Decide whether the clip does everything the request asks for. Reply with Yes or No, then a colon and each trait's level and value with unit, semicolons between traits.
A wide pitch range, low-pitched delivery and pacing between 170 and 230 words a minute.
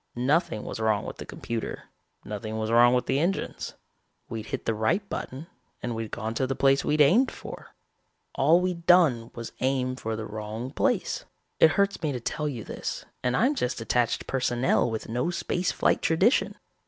Yes: wide, 6.0 semitones; low, 125 Hz; average, 185 wpm